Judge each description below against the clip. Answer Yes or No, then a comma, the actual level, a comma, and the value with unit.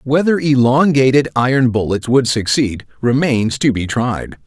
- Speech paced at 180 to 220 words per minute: No, slow, 135 wpm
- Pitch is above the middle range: No, low, 125 Hz